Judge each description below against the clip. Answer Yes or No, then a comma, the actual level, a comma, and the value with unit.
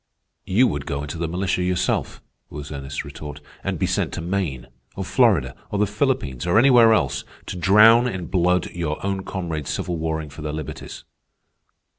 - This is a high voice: No, very low, 85 Hz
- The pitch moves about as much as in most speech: Yes, average, 4.8 semitones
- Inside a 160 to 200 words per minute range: Yes, average, 175 wpm